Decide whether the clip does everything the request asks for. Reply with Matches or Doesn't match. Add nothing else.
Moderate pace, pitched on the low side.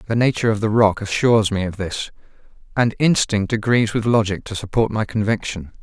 Matches